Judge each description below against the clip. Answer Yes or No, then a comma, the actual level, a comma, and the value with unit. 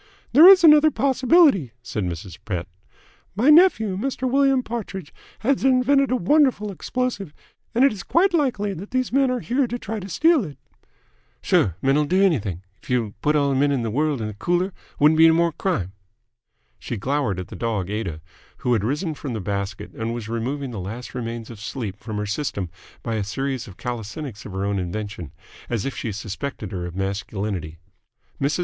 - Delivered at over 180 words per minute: Yes, average, 195 wpm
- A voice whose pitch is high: No, medium, 140 Hz